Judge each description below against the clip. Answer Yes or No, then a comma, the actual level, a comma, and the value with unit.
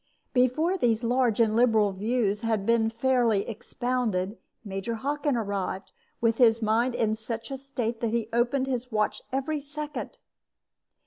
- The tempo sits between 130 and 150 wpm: Yes, average, 145 wpm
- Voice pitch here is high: Yes, high, 235 Hz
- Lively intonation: No, average, 2.8 semitones